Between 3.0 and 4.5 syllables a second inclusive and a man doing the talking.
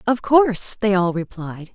No: 4.4 syllables/s; female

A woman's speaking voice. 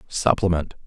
No: male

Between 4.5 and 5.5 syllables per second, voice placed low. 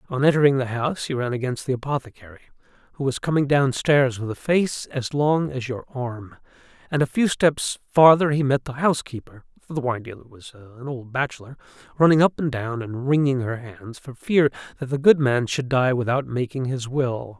Yes: 5.4 syllables/s; low, 130 Hz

